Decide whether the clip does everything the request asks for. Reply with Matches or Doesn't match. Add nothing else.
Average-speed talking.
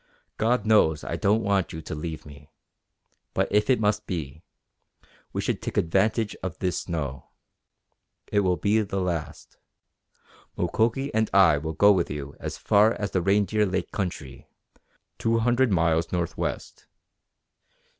Matches